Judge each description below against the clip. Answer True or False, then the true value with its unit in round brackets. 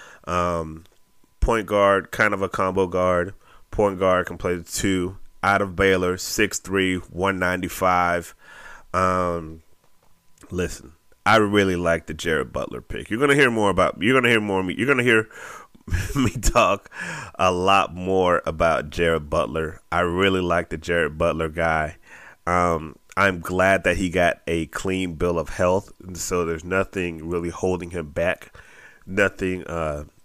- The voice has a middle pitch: False (90 Hz)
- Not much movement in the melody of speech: True (2.1 semitones)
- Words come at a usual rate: True (160 wpm)